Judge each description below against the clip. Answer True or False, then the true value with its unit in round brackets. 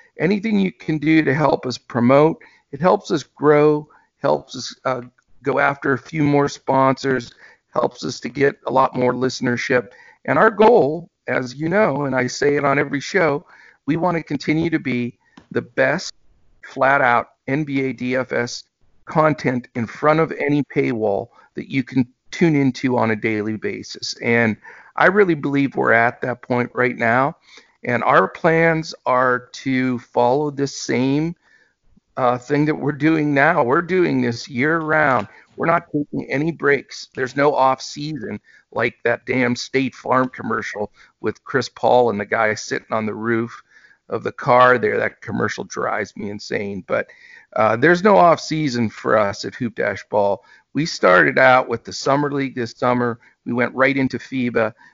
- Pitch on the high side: False (135 Hz)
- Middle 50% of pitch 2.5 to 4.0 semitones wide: True (3.3 semitones)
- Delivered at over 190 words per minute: False (175 wpm)